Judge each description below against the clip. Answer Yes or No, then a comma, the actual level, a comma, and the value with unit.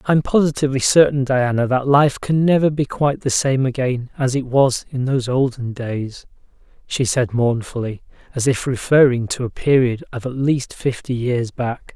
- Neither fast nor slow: Yes, average, 175 wpm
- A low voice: Yes, low, 130 Hz